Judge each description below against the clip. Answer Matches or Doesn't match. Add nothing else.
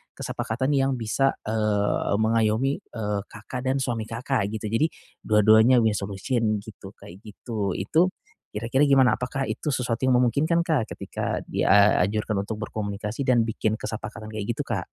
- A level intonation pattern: Doesn't match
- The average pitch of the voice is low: Matches